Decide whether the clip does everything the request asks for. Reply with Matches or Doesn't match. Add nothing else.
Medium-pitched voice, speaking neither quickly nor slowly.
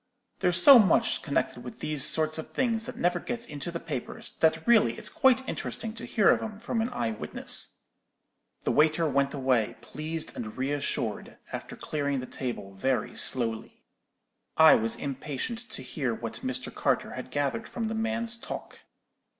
Matches